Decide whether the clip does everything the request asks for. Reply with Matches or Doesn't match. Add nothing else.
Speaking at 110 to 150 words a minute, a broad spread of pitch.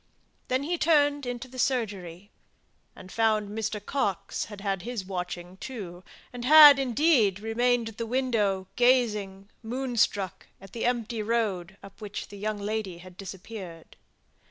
Doesn't match